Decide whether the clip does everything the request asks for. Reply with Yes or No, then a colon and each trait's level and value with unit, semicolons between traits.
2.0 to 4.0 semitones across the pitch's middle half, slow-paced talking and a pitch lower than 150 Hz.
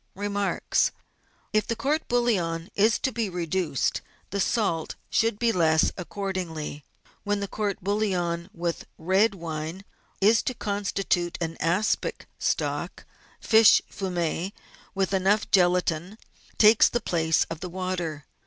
No: average, 3.5 semitones; slow, 130 wpm; high, 190 Hz